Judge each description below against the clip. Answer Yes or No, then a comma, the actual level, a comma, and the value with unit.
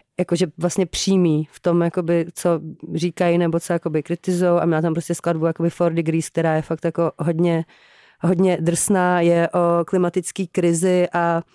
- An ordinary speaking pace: Yes, average, 160 wpm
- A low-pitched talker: No, medium, 170 Hz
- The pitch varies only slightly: Yes, narrow, 1.1 semitones